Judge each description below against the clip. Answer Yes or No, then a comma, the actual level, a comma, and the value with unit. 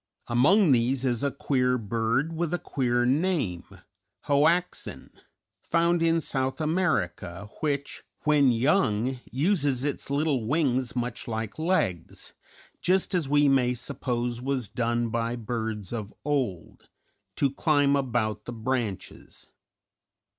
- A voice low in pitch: Yes, low, 130 Hz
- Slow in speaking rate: Yes, slow, 120 wpm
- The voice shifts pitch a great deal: No, average, 4.2 semitones